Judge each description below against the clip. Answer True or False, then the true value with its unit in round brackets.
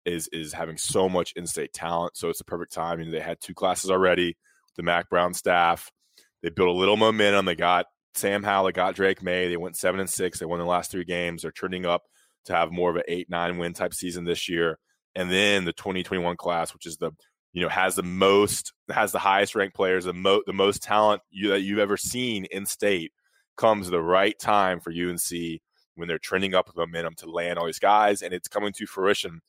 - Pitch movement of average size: False (2.2 semitones)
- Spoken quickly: True (235 wpm)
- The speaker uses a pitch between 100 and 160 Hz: False (90 Hz)